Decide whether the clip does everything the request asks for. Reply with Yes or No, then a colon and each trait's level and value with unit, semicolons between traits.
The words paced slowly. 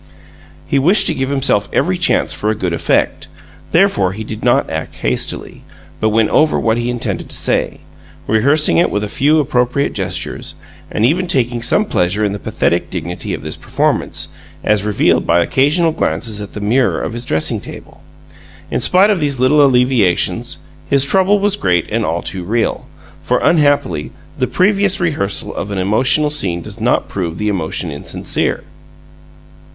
No: average, 170 wpm